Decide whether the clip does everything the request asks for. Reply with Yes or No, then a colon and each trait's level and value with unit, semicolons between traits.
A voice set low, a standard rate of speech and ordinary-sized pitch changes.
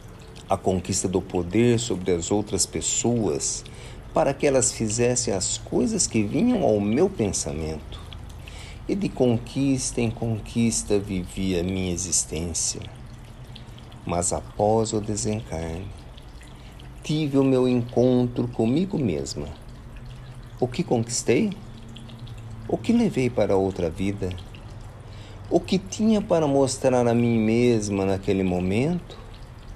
No: low, 115 Hz; slow, 115 wpm; average, 3.9 semitones